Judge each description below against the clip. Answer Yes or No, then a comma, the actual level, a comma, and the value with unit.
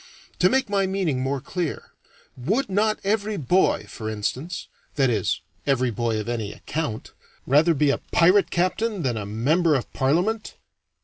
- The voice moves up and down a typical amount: No, wide, 7.6 semitones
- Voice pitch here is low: No, medium, 155 Hz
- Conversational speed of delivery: Yes, average, 160 wpm